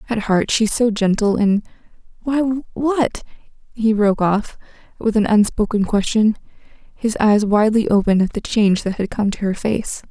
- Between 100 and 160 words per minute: Yes, average, 155 wpm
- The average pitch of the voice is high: Yes, high, 215 Hz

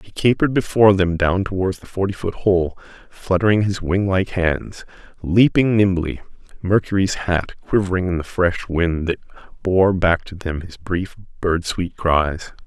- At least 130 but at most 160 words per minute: Yes, average, 145 wpm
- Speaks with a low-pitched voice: Yes, very low, 90 Hz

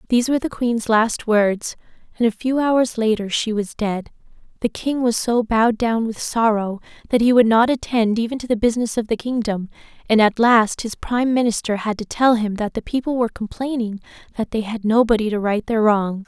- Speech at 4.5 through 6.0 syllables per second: Yes, 5.4 syllables/s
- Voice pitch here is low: No, high, 225 Hz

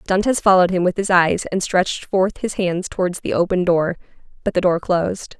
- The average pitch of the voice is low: No, medium, 185 Hz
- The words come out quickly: Yes, fast, 210 wpm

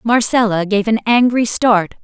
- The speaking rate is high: No, average, 150 wpm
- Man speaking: No, female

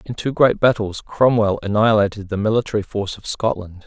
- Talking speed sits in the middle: Yes, average, 170 wpm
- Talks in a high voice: No, low, 105 Hz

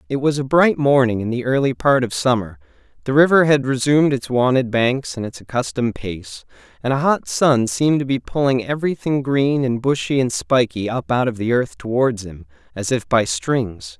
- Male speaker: Yes, male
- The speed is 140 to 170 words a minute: No, average, 200 wpm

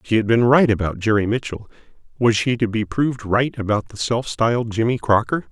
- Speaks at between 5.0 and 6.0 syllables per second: Yes, 5.5 syllables/s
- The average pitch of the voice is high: No, low, 115 Hz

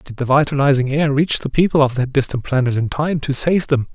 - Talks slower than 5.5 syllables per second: No, 5.7 syllables/s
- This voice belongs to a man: Yes, male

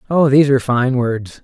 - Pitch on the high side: No, low, 130 Hz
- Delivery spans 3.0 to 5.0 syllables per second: No, 5.7 syllables/s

